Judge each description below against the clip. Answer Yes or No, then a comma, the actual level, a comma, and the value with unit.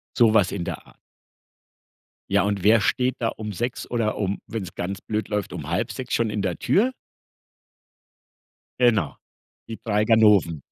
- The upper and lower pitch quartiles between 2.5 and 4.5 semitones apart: Yes, average, 2.8 semitones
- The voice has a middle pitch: No, low, 105 Hz